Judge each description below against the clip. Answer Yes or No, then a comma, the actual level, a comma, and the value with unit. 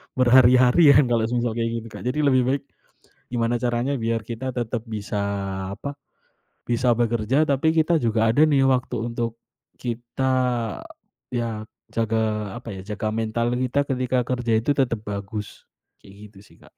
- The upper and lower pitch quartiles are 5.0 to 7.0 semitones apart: No, narrow, 2.4 semitones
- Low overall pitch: Yes, low, 120 Hz